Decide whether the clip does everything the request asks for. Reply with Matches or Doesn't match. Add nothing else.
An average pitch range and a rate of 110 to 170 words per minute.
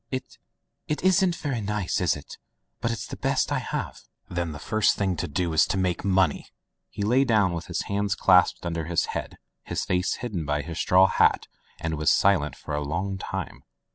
Doesn't match